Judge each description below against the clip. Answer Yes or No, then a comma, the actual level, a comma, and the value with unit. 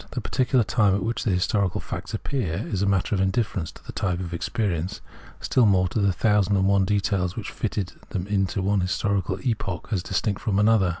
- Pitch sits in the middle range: No, low, 100 Hz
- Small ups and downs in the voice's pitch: Yes, narrow, 2.1 semitones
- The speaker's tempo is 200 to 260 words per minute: Yes, fast, 205 wpm